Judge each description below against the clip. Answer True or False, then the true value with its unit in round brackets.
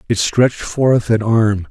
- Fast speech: False (175 wpm)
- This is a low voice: True (115 Hz)